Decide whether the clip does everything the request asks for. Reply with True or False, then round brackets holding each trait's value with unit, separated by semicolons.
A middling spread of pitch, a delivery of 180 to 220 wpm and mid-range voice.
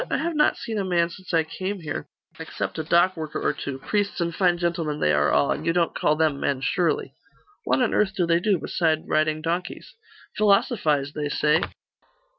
True (3.5 semitones; 205 wpm; 170 Hz)